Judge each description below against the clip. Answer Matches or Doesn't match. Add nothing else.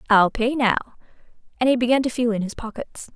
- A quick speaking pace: Matches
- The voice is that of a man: Doesn't match